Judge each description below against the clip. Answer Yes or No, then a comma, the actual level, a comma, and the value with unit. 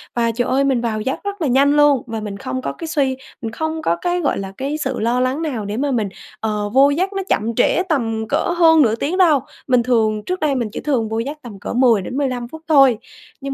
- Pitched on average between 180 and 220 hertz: No, very high, 260 Hz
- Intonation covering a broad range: No, average, 4.5 semitones